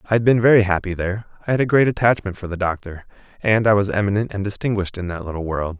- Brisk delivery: Yes, fast, 250 wpm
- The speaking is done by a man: Yes, male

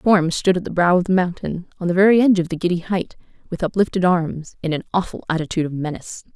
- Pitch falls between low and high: Yes, medium, 175 Hz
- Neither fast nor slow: No, fast, 245 wpm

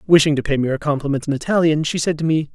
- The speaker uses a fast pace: Yes, fast, 285 wpm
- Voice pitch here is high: No, medium, 150 Hz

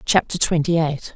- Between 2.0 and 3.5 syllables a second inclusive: No, 4.8 syllables/s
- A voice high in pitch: No, medium, 160 Hz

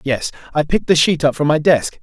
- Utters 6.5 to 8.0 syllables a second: No, 5.9 syllables/s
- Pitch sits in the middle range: Yes, medium, 150 Hz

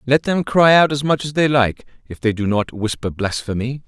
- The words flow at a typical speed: No, fast, 230 wpm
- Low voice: Yes, low, 125 Hz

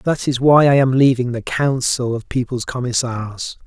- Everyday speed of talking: Yes, average, 180 wpm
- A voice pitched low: Yes, low, 125 Hz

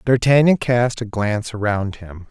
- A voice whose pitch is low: Yes, low, 115 Hz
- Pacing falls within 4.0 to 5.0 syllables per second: Yes, 4.6 syllables/s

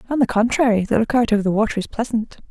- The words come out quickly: Yes, fast, 265 wpm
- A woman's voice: Yes, female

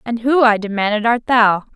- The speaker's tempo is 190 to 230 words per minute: Yes, fast, 205 wpm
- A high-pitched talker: Yes, high, 225 Hz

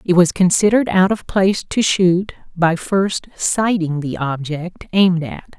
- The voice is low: No, medium, 180 Hz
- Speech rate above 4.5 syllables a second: No, 4.3 syllables/s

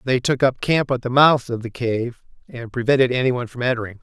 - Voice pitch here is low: Yes, low, 125 Hz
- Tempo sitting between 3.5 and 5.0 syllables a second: No, 6.2 syllables/s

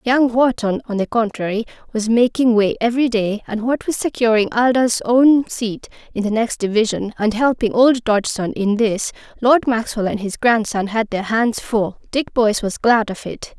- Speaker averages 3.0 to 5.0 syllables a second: Yes, 4.7 syllables/s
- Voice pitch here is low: No, high, 230 Hz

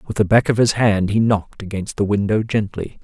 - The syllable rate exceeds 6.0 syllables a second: No, 5.6 syllables/s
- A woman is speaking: No, male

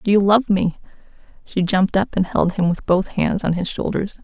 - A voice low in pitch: No, high, 190 Hz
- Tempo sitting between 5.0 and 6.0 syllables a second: Yes, 5.2 syllables/s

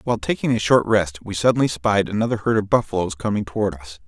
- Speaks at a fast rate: Yes, fast, 220 wpm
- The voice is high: No, low, 100 Hz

